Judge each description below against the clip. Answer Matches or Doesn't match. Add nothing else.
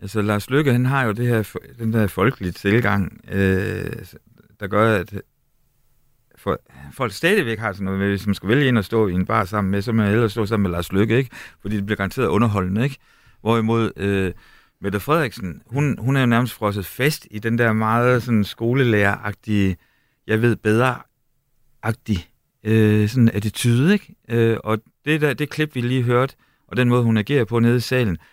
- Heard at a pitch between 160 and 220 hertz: Doesn't match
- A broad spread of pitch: Doesn't match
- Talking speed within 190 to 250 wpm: Matches